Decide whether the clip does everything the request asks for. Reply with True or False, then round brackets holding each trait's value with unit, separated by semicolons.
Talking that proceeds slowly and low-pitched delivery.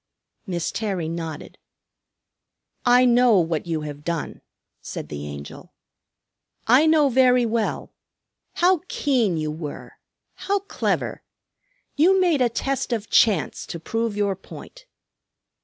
False (125 wpm; 225 Hz)